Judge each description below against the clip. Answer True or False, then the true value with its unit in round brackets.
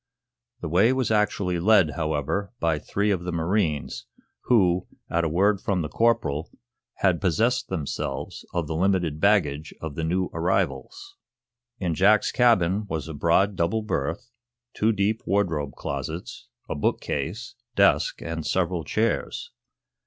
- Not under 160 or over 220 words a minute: False (145 wpm)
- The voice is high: False (90 Hz)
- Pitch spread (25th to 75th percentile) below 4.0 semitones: False (4.3 semitones)